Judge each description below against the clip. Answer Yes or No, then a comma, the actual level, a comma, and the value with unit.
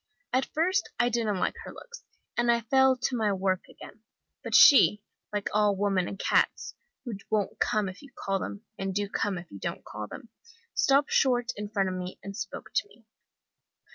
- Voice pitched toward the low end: No, high, 210 Hz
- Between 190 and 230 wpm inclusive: Yes, average, 200 wpm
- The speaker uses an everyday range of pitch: Yes, average, 4.4 semitones